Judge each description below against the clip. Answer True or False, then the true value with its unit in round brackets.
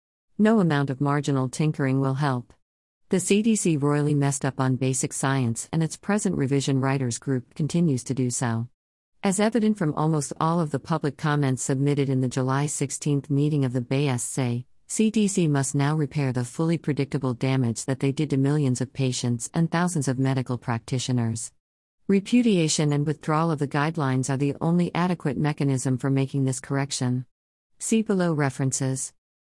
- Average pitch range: True (3.0 semitones)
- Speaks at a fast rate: False (165 wpm)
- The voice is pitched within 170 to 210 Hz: False (140 Hz)